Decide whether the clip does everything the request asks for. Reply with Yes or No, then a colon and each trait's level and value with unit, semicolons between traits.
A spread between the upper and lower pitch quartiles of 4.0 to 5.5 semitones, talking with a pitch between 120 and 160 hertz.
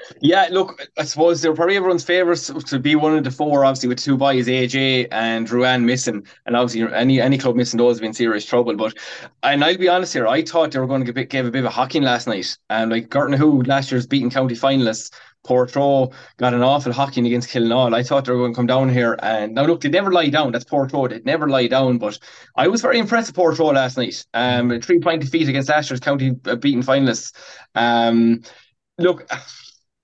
No: average, 3.3 semitones; low, 130 Hz